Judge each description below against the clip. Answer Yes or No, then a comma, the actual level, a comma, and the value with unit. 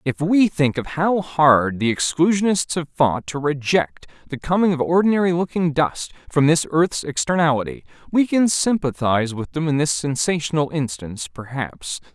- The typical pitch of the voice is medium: Yes, medium, 150 Hz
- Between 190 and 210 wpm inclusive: No, average, 160 wpm